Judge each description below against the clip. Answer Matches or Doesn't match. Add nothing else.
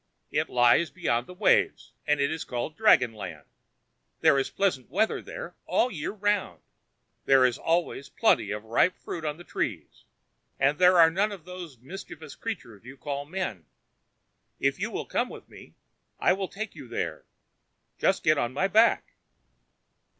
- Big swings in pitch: Matches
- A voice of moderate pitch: Matches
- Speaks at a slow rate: Doesn't match